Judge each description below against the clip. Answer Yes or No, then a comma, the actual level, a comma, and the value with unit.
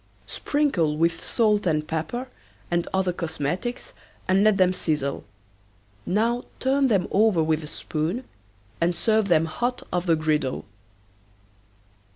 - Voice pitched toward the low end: No, medium, 180 Hz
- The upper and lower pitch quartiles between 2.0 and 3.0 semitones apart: No, wide, 5.6 semitones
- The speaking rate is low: Yes, slow, 130 wpm